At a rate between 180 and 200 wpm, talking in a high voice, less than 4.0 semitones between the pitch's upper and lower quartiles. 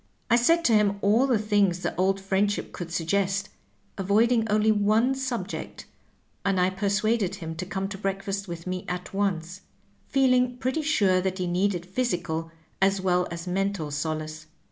No: average, 165 wpm; high, 195 Hz; average, 3.1 semitones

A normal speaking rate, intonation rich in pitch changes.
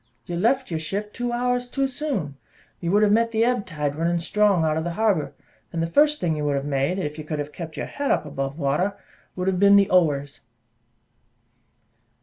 No: fast, 215 wpm; wide, 6.2 semitones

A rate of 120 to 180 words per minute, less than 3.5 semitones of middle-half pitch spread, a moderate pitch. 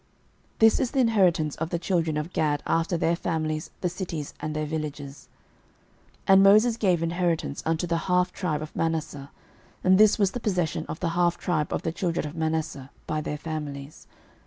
No: average, 190 wpm; average, 2.8 semitones; medium, 165 Hz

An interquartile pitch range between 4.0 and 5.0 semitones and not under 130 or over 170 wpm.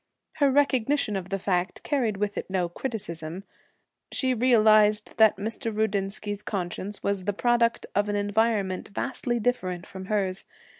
No: average, 3.2 semitones; average, 145 wpm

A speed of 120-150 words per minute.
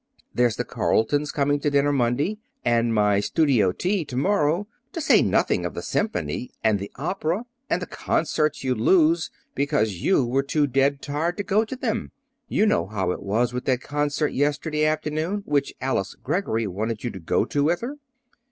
No: average, 185 wpm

